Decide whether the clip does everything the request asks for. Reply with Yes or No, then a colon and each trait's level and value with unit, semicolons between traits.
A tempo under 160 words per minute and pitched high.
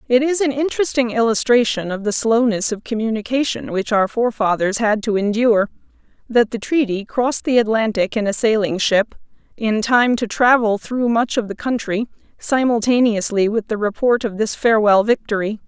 No: average, 165 wpm; high, 225 Hz